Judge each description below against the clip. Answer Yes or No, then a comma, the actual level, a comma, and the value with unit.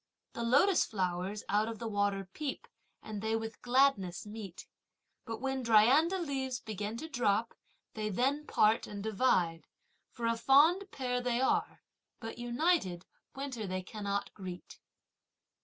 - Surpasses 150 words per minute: No, average, 140 wpm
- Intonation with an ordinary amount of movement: Yes, average, 4.5 semitones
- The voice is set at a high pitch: Yes, high, 225 Hz